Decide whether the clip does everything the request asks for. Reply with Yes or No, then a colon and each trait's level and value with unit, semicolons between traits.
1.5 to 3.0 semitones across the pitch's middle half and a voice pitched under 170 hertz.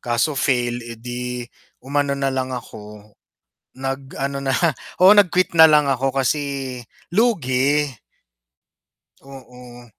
Yes: average, 2.7 semitones; low, 135 Hz